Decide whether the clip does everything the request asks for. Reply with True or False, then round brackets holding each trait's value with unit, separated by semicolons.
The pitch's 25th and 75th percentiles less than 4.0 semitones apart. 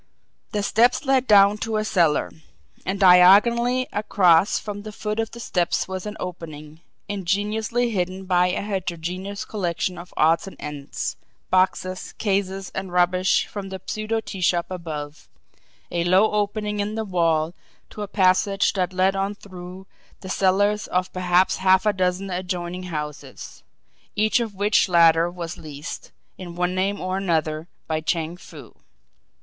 True (2.7 semitones)